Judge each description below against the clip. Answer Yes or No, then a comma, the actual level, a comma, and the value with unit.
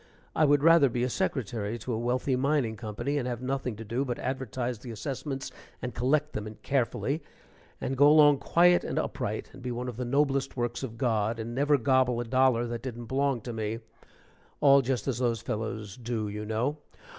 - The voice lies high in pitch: No, low, 125 Hz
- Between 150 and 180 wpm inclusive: No, average, 200 wpm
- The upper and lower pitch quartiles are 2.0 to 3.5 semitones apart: Yes, average, 3.1 semitones